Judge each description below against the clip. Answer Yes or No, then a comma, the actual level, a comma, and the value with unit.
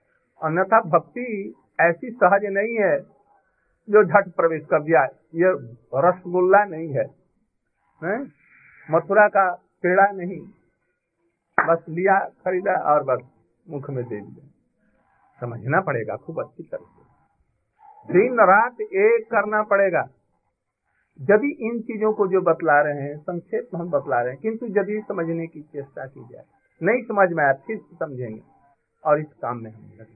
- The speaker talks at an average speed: Yes, average, 140 wpm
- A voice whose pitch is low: No, medium, 180 Hz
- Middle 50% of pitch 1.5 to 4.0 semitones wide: No, average, 5.3 semitones